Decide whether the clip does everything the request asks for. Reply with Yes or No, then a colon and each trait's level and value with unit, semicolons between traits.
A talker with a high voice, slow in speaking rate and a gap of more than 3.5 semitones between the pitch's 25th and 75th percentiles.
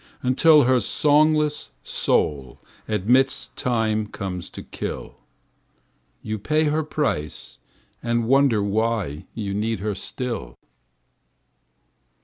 No: low, 115 Hz; slow, 100 wpm; average, 5.1 semitones